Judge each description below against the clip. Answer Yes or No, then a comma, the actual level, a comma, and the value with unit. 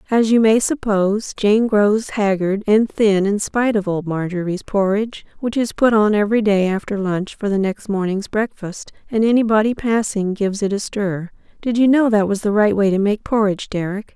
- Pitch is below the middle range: No, high, 210 Hz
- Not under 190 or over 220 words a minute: Yes, average, 195 wpm